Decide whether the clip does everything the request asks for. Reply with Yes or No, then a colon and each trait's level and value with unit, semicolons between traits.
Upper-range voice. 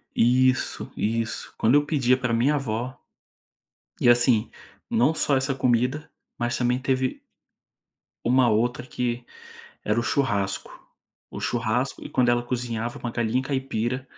No: low, 125 Hz